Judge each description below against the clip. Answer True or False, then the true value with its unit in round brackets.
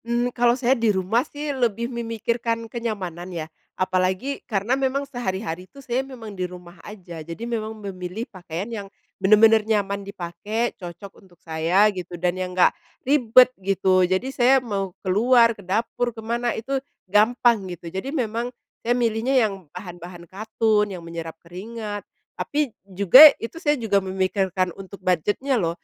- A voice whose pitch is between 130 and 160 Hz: False (210 Hz)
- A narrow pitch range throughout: False (4.4 semitones)